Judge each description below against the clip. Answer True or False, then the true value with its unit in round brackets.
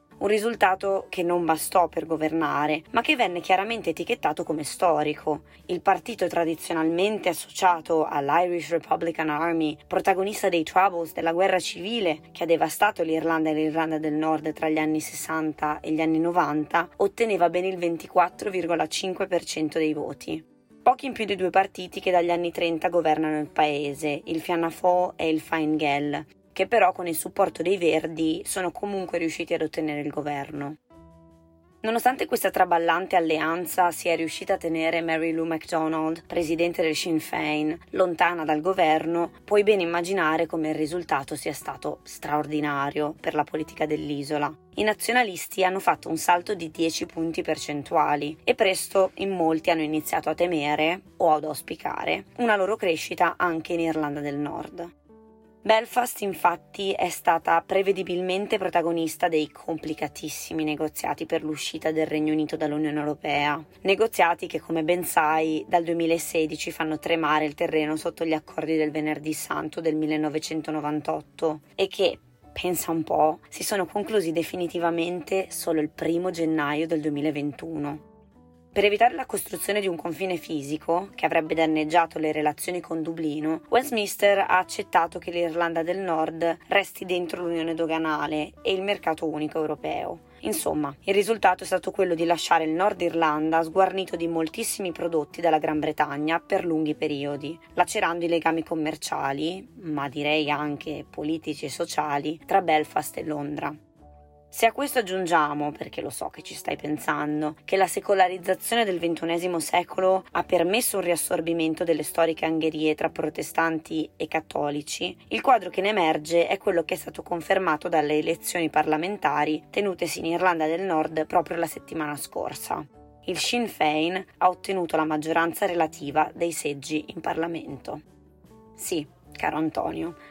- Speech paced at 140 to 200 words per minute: True (150 wpm)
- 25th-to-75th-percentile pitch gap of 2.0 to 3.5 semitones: True (2.7 semitones)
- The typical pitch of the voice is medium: True (165 Hz)